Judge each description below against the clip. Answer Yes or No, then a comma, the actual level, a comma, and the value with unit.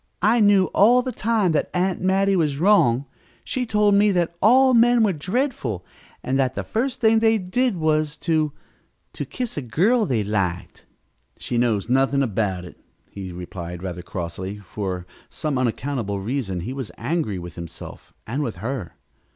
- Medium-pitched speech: Yes, medium, 145 Hz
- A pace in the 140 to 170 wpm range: Yes, average, 165 wpm